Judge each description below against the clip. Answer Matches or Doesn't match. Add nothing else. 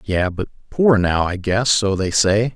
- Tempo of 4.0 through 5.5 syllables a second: Matches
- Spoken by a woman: Doesn't match